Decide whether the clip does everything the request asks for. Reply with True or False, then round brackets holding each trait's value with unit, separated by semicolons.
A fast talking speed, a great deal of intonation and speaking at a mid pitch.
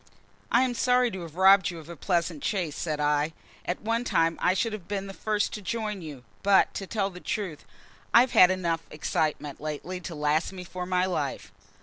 False (215 wpm; 4.2 semitones; 180 Hz)